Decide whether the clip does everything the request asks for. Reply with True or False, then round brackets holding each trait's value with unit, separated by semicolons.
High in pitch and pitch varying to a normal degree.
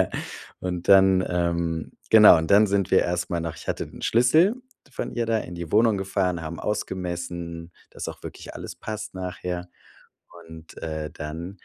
False (90 Hz; 3.0 semitones)